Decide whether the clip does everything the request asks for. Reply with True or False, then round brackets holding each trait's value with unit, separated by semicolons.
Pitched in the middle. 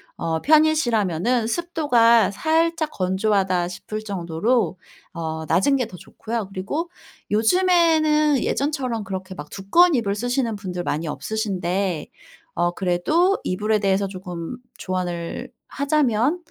False (215 Hz)